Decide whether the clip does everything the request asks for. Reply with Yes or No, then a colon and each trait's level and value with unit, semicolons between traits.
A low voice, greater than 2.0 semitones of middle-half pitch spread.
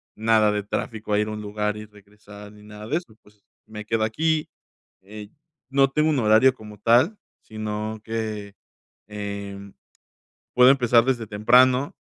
Yes: low, 110 Hz; average, 2.7 semitones